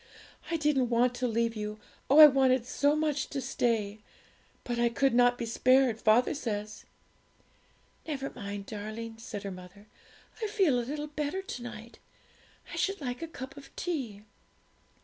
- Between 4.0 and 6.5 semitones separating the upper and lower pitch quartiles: Yes, average, 4.3 semitones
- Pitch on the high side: Yes, high, 245 Hz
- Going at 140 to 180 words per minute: Yes, average, 165 wpm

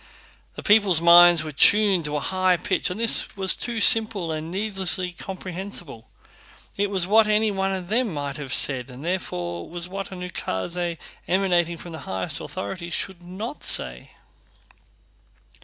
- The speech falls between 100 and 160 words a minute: Yes, average, 155 wpm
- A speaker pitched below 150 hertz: No, medium, 180 Hz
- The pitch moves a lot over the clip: No, average, 3.3 semitones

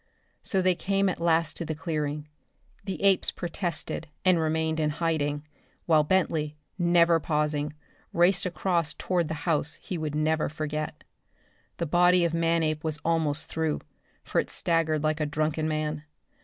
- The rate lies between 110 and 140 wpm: No, average, 155 wpm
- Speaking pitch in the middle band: Yes, medium, 160 Hz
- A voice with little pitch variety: Yes, narrow, 2.0 semitones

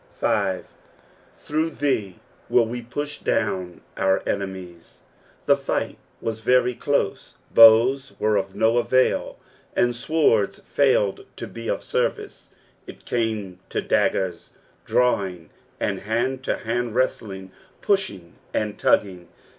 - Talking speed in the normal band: No, slow, 125 wpm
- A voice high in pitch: No, low, 110 Hz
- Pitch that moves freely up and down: No, average, 4.6 semitones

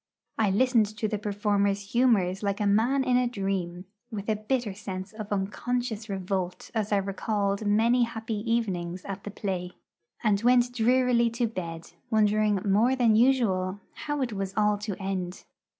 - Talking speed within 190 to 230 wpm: No, average, 165 wpm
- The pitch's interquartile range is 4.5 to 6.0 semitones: No, average, 3.1 semitones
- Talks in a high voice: Yes, high, 210 Hz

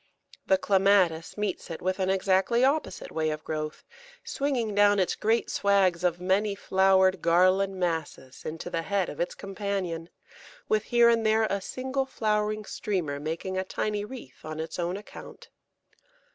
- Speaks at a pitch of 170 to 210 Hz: Yes, high, 190 Hz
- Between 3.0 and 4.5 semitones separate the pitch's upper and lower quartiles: Yes, average, 3.5 semitones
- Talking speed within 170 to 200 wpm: No, average, 160 wpm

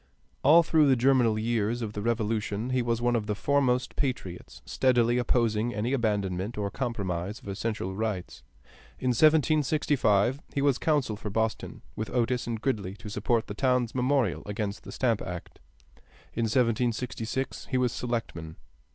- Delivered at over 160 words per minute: No, average, 155 wpm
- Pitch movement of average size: Yes, average, 3.3 semitones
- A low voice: Yes, low, 115 Hz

